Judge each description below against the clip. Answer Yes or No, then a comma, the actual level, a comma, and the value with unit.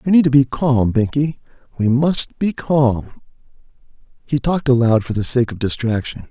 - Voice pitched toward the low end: Yes, low, 130 Hz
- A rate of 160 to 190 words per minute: Yes, average, 170 wpm